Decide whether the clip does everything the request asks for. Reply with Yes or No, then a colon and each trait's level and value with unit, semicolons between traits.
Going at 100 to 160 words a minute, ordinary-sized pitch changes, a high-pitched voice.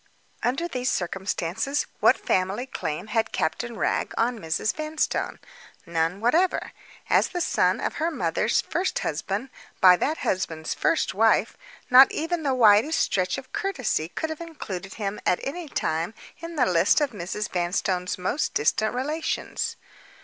No: average, 150 wpm; wide, 8.7 semitones; high, 220 Hz